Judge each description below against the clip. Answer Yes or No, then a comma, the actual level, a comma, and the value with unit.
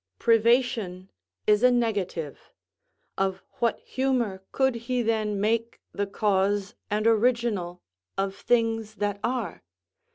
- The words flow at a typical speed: No, slow, 110 wpm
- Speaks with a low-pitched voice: No, high, 215 Hz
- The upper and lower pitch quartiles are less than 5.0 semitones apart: Yes, average, 3.1 semitones